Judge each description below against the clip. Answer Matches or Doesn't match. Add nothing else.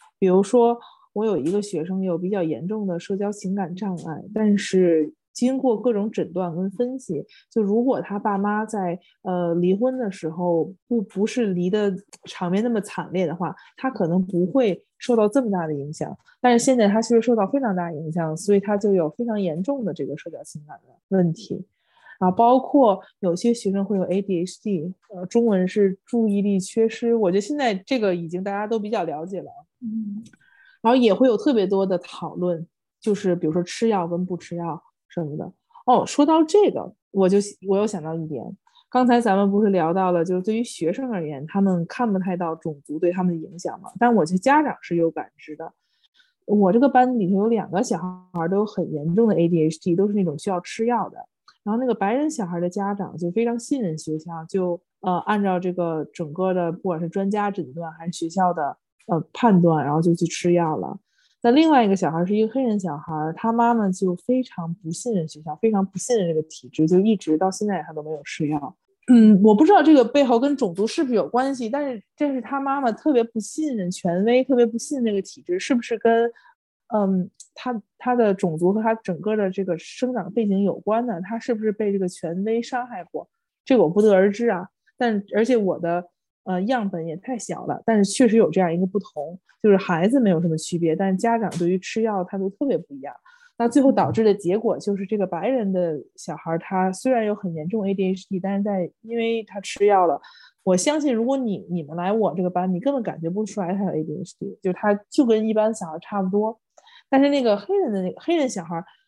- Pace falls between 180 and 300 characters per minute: Doesn't match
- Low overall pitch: Doesn't match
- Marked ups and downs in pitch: Doesn't match